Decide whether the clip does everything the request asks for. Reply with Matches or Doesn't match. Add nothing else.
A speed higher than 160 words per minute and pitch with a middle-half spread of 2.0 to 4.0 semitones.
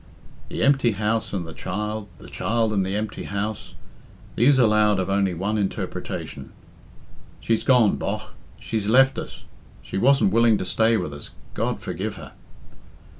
Doesn't match